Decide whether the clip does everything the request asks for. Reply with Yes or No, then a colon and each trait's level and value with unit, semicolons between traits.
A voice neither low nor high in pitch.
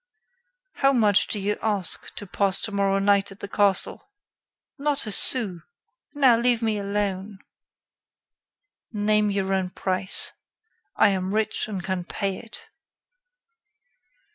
No: high, 200 Hz